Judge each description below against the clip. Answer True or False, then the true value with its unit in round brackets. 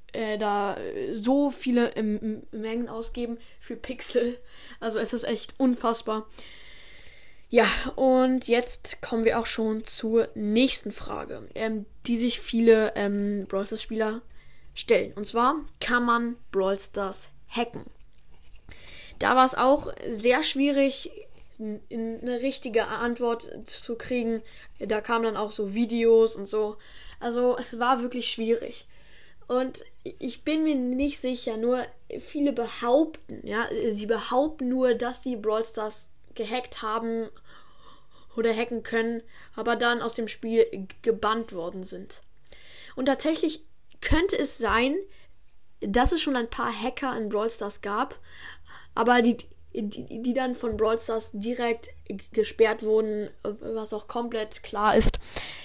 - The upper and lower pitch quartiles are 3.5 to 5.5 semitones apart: False (2.4 semitones)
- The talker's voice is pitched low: False (230 Hz)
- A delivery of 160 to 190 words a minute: False (140 wpm)